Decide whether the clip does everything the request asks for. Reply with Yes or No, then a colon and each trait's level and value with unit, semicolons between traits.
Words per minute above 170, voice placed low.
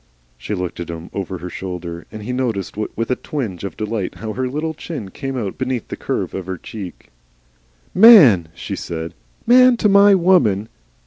Yes: average, 185 wpm; low, 110 Hz